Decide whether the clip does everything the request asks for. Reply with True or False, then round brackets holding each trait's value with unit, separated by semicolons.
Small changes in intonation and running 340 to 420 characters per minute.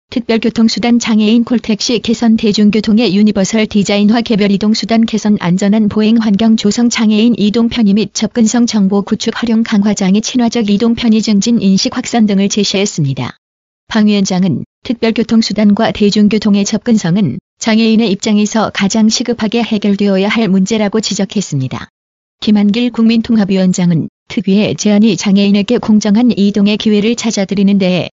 True (2.0 semitones; 375 characters per minute)